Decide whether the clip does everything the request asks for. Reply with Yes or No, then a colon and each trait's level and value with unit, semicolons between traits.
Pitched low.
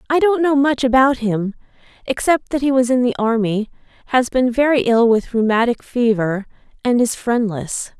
No: high, 245 Hz